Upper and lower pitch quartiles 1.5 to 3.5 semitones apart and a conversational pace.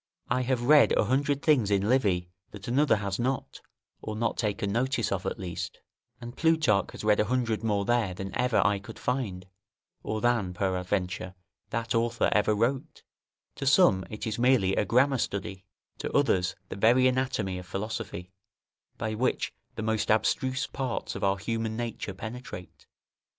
No: average, 4.3 semitones; average, 165 wpm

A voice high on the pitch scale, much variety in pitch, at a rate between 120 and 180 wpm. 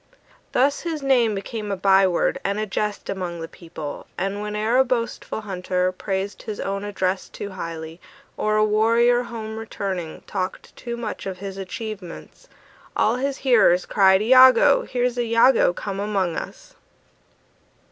No: high, 210 Hz; average, 3.6 semitones; average, 150 wpm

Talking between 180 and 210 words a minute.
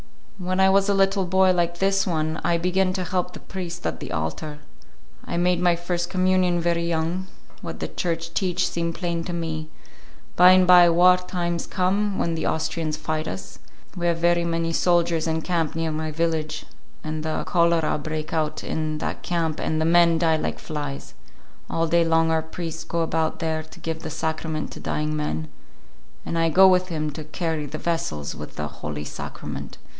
Yes: average, 190 wpm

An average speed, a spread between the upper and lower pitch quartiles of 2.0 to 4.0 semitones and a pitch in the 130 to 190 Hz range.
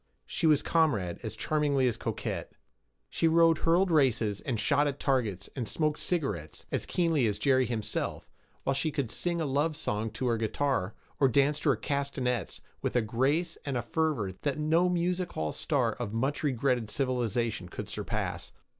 No: average, 180 wpm; average, 5.2 semitones; low, 135 Hz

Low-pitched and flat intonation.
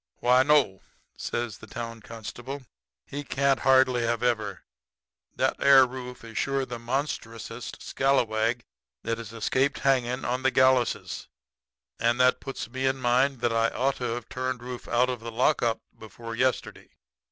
Yes: low, 125 Hz; narrow, 2.3 semitones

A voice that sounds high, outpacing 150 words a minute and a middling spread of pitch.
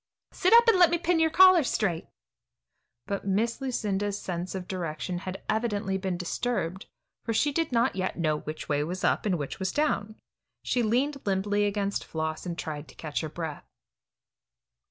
No: high, 200 Hz; average, 175 wpm; wide, 5.8 semitones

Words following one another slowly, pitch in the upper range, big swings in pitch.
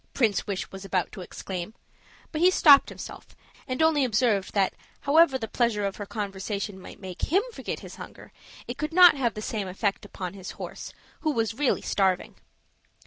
No: average, 185 wpm; high, 215 Hz; wide, 6.0 semitones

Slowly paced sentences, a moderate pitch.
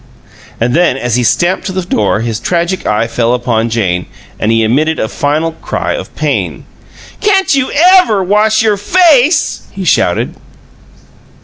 No: average, 155 wpm; medium, 160 Hz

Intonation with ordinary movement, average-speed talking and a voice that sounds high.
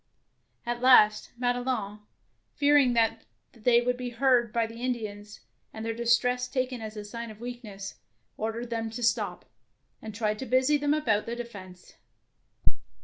No: narrow, 2.3 semitones; average, 155 wpm; high, 235 Hz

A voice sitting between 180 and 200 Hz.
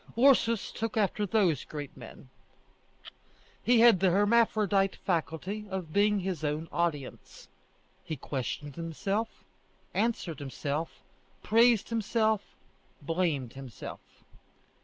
Yes: high, 190 Hz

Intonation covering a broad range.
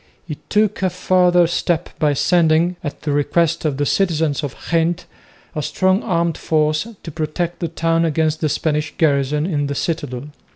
No: narrow, 2.5 semitones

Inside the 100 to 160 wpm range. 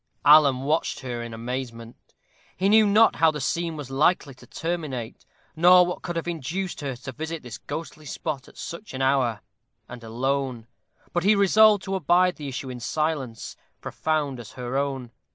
No: average, 175 wpm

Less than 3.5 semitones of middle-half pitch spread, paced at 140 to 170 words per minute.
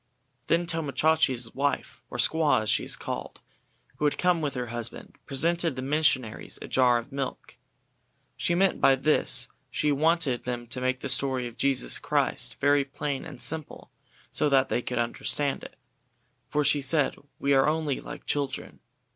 No: average, 2.9 semitones; average, 180 wpm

